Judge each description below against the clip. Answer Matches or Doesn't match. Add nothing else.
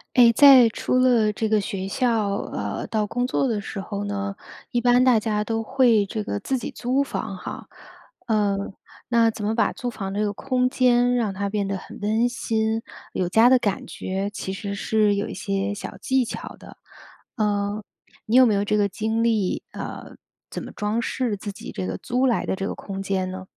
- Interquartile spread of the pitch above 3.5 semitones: Doesn't match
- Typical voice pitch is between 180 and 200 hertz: Doesn't match